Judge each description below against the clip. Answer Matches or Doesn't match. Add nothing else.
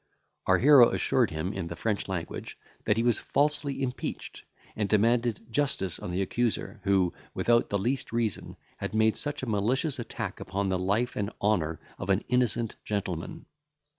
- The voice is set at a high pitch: Doesn't match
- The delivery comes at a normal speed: Matches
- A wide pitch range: Doesn't match